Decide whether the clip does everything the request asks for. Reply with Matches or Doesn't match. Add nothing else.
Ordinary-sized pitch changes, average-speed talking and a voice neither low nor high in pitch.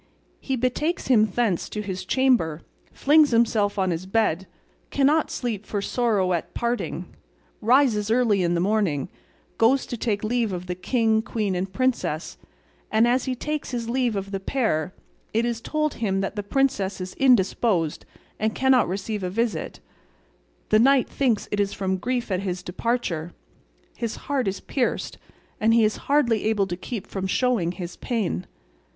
Doesn't match